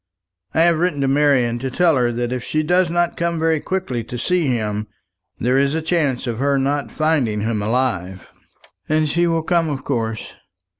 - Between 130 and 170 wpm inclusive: No, average, 195 wpm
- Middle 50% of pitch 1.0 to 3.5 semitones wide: No, average, 5.2 semitones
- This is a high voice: No, medium, 140 Hz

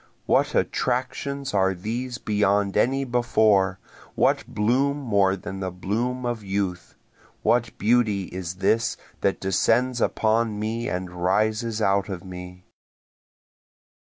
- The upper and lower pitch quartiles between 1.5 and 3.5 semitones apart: No, average, 3.9 semitones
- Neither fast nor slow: No, slow, 120 wpm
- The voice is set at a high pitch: No, low, 105 Hz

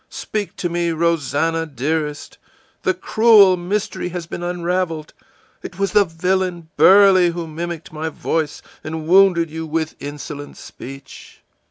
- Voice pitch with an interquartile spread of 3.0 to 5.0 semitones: No, narrow, 2.6 semitones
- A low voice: No, medium, 170 Hz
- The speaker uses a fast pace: No, slow, 135 wpm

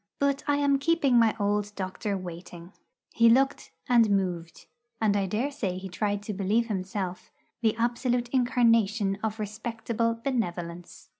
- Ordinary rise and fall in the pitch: Yes, average, 3.7 semitones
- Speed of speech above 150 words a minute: No, average, 140 wpm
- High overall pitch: Yes, high, 215 Hz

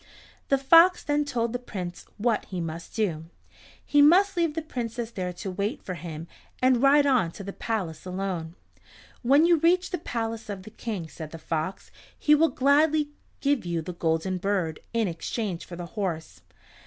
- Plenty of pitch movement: Yes, wide, 8.3 semitones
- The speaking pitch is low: No, high, 220 Hz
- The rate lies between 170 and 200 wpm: Yes, average, 180 wpm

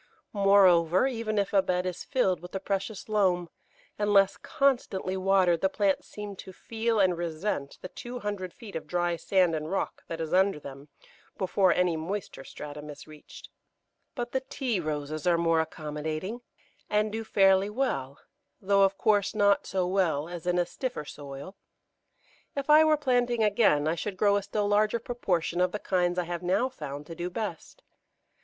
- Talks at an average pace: Yes, average, 175 wpm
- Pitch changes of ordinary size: Yes, average, 3.8 semitones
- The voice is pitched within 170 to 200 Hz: Yes, high, 190 Hz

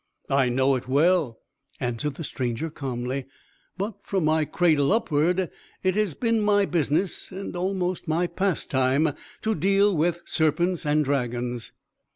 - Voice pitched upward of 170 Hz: No, medium, 160 Hz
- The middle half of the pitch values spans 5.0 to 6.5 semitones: Yes, wide, 5.5 semitones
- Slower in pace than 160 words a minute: Yes, average, 140 wpm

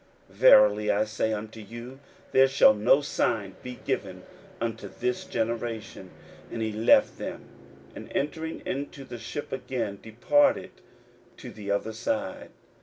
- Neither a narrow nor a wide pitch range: Yes, average, 3.9 semitones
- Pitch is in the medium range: No, low, 115 Hz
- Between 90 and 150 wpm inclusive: Yes, average, 140 wpm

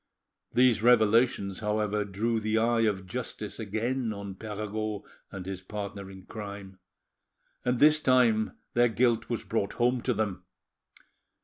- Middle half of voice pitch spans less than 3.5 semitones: Yes, average, 2.8 semitones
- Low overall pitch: Yes, low, 110 Hz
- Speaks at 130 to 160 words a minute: Yes, slow, 135 wpm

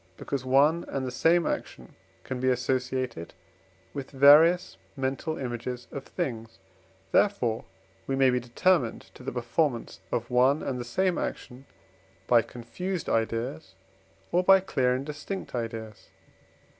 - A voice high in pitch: No, low, 130 Hz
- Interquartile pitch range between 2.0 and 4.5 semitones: Yes, average, 4.1 semitones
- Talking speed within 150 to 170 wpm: No, slow, 135 wpm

